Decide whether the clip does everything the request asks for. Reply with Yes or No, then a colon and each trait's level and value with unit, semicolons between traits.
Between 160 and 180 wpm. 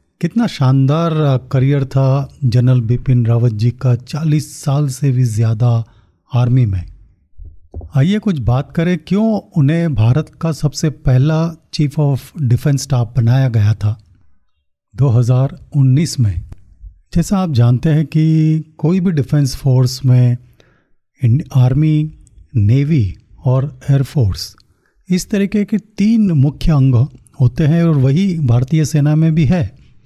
No: average, 130 wpm